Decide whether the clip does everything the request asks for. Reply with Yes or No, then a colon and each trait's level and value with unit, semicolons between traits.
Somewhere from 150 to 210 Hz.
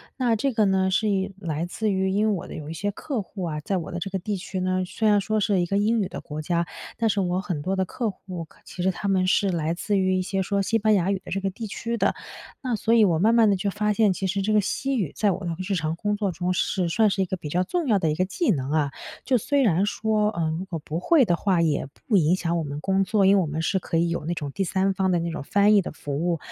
Yes: high, 190 Hz